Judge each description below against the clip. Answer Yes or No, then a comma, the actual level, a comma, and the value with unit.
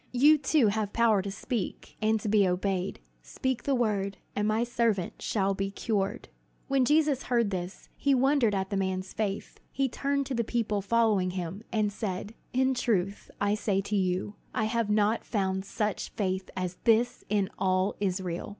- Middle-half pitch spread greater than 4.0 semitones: No, average, 3.4 semitones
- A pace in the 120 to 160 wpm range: No, average, 175 wpm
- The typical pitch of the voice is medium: No, high, 210 Hz